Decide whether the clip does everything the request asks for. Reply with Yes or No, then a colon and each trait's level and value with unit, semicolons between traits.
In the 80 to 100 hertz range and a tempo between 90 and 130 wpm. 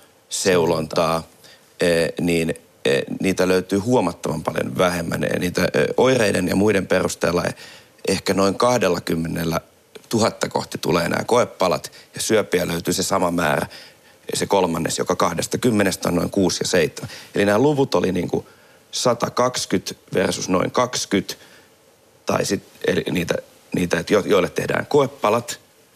Yes: very low, 95 Hz; average, 125 wpm